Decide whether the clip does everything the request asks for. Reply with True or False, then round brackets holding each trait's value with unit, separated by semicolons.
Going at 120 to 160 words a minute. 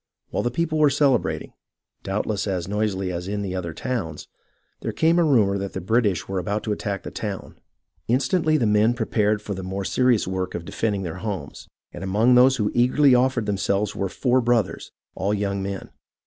False (190 wpm)